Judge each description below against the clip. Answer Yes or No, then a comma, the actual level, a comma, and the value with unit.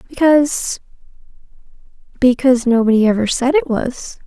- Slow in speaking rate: Yes, slow, 85 wpm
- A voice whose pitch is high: Yes, very high, 255 Hz